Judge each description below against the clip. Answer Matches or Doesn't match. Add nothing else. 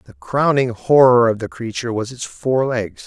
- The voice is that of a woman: Doesn't match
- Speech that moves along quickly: Doesn't match